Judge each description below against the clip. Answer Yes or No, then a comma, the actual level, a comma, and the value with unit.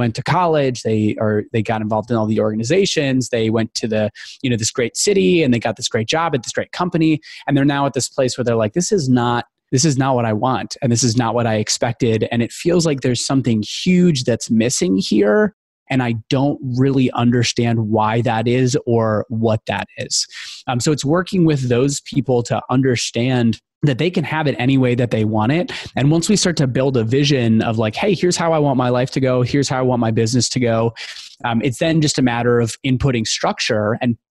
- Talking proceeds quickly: Yes, fast, 235 wpm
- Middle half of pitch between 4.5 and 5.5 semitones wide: No, average, 3.6 semitones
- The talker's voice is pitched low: Yes, low, 125 Hz